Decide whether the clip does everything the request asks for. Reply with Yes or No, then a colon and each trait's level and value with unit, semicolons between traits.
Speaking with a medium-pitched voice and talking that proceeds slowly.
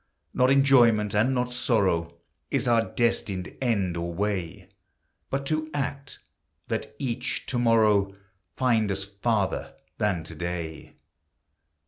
No: low, 110 Hz; slow, 120 wpm